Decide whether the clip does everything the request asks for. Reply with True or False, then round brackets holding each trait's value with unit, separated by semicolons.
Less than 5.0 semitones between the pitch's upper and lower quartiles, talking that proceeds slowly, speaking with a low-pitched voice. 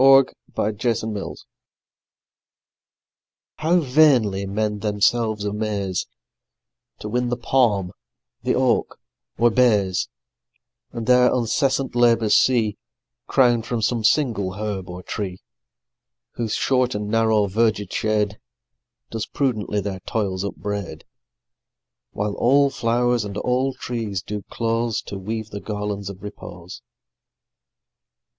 True (3.0 semitones; 115 wpm; 110 Hz)